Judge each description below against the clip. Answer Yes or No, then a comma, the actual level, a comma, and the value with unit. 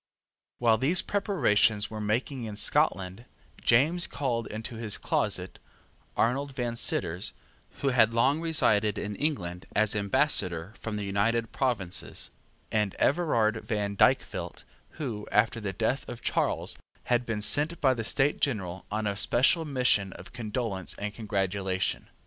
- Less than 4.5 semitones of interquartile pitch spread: Yes, average, 4.1 semitones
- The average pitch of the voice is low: Yes, low, 110 Hz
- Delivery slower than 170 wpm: Yes, average, 140 wpm